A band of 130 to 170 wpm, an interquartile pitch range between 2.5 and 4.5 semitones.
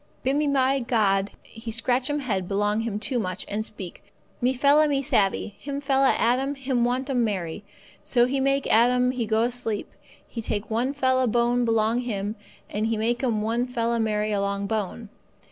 No: average, 180 wpm; average, 3.3 semitones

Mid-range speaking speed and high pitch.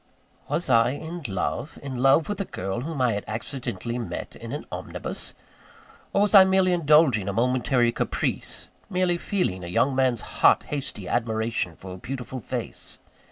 No: average, 165 wpm; low, 130 Hz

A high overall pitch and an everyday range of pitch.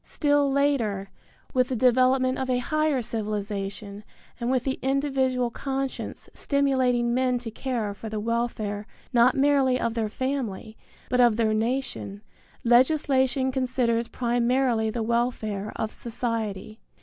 Yes: high, 245 Hz; average, 3.1 semitones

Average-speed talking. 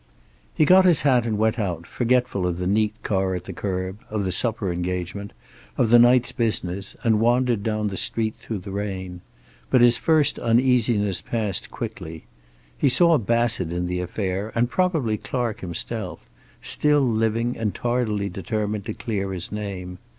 Yes: average, 165 wpm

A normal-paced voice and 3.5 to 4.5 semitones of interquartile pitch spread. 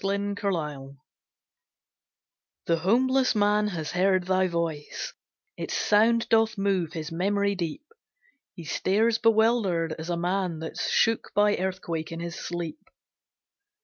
No: slow, 130 wpm; average, 3.8 semitones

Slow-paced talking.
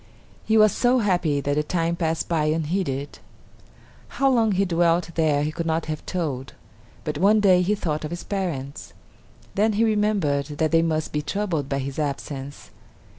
No: average, 180 wpm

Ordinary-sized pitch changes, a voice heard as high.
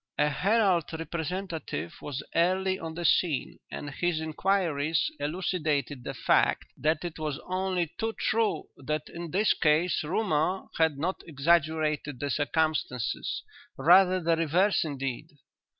No: average, 3.5 semitones; medium, 160 Hz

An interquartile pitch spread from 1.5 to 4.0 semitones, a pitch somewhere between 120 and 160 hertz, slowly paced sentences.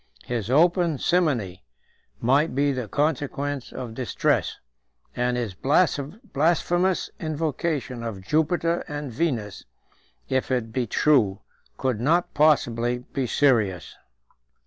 No: average, 4.6 semitones; low, 135 Hz; slow, 105 wpm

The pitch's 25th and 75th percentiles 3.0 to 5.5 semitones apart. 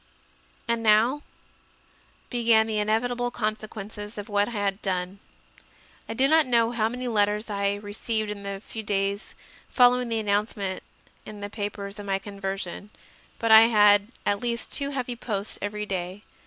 No: narrow, 2.4 semitones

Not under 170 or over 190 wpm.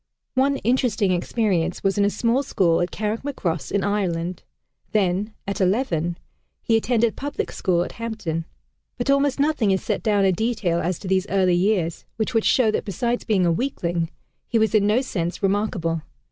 Yes: average, 175 wpm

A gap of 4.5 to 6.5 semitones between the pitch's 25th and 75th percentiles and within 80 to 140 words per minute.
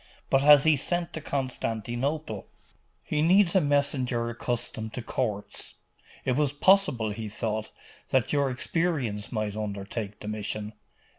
Yes: average, 5.3 semitones; slow, 135 wpm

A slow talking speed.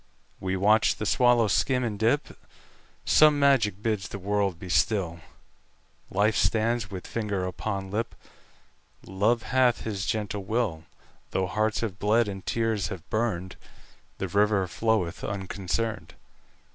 Yes: slow, 115 wpm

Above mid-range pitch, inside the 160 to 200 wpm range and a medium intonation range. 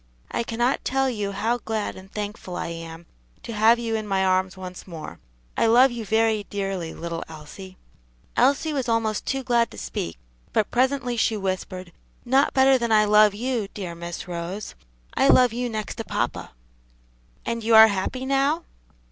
Yes: high, 215 Hz; average, 180 wpm; average, 4.3 semitones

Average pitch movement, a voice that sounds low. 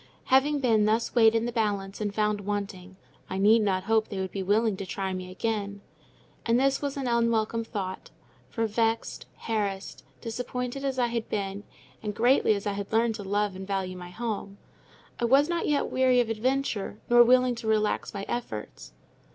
No: average, 3.1 semitones; high, 220 Hz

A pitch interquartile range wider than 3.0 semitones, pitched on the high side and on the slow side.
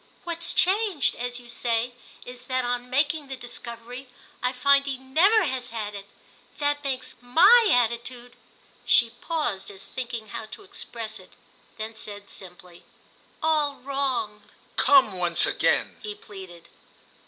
Yes: average, 4.1 semitones; very high, 250 Hz; slow, 130 wpm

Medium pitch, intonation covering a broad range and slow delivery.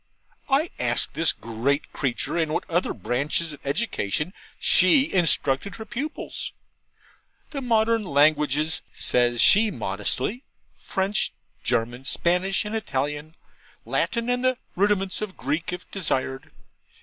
Yes: medium, 170 Hz; wide, 7.3 semitones; slow, 120 wpm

